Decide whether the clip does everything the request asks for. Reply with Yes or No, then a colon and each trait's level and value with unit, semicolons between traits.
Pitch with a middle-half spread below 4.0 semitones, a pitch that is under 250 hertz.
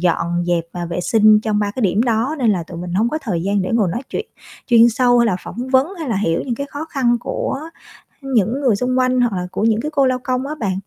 No: average, 4.8 semitones; high, 230 Hz